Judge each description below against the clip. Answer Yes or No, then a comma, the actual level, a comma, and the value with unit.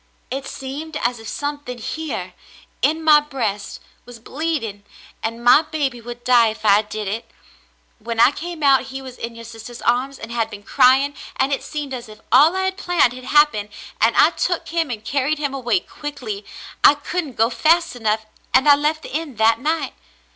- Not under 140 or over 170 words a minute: No, average, 195 wpm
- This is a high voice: Yes, very high, 260 Hz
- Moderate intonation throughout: Yes, average, 4.6 semitones